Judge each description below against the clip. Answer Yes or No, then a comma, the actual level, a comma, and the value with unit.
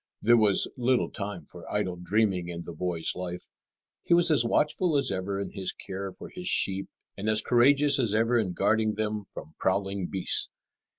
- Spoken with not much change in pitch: No, average, 4.2 semitones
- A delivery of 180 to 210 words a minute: Yes, average, 185 wpm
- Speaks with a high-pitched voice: No, low, 100 Hz